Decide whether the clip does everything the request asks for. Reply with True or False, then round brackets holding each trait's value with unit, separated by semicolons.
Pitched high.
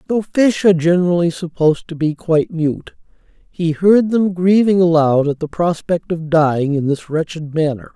False (165 Hz)